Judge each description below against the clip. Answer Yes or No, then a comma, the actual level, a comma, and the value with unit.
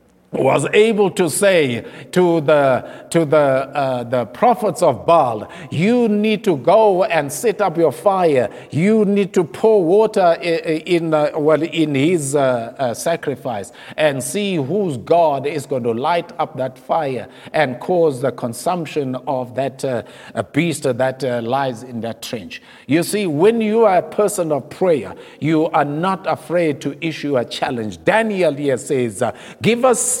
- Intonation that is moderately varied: No, wide, 6.1 semitones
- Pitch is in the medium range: Yes, medium, 155 Hz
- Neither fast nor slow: Yes, average, 165 wpm